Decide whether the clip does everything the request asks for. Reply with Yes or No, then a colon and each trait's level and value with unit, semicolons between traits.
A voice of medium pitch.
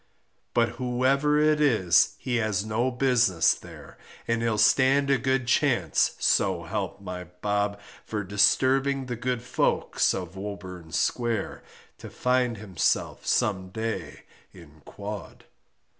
No: low, 115 Hz